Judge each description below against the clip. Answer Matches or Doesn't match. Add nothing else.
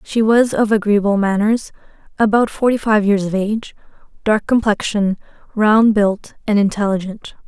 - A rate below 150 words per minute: Matches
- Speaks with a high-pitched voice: Matches